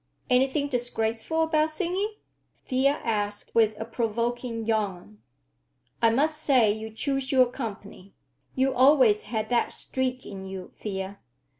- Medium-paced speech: No, slow, 130 wpm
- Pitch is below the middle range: No, high, 235 Hz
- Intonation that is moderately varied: Yes, average, 4.0 semitones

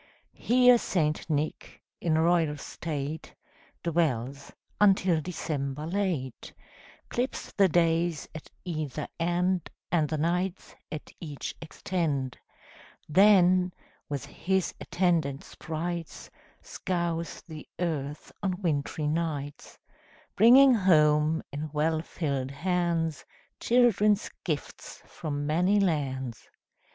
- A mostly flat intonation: No, average, 3.3 semitones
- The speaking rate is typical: No, slow, 100 wpm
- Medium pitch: Yes, medium, 165 Hz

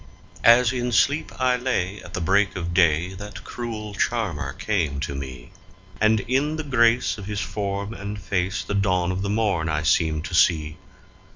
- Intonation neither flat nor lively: Yes, average, 4.1 semitones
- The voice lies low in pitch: Yes, low, 100 Hz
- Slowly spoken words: No, average, 175 wpm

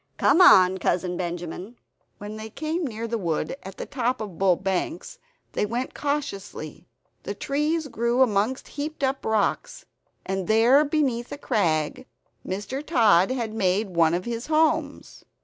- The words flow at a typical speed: Yes, average, 150 wpm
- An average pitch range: No, wide, 6.2 semitones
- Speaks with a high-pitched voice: Yes, high, 220 Hz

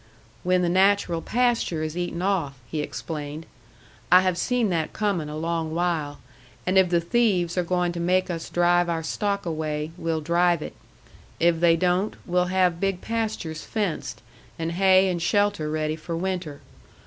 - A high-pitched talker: No, medium, 175 Hz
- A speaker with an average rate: Yes, average, 170 wpm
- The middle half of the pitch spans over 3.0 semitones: No, narrow, 2.4 semitones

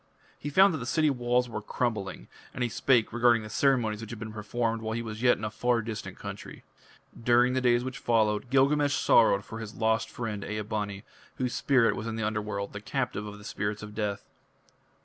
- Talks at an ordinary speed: No, fast, 210 wpm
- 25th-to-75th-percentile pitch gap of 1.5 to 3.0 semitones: Yes, narrow, 2.6 semitones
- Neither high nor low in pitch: No, low, 115 Hz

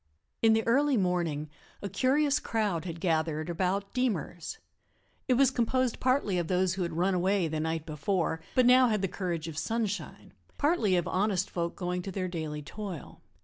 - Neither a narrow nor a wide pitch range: Yes, average, 5.0 semitones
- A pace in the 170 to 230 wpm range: Yes, average, 180 wpm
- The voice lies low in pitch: No, medium, 185 Hz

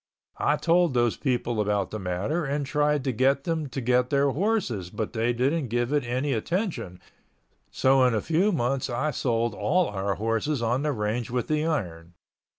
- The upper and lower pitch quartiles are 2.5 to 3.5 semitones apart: No, average, 4.8 semitones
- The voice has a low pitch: Yes, low, 125 Hz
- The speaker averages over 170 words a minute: Yes, average, 185 wpm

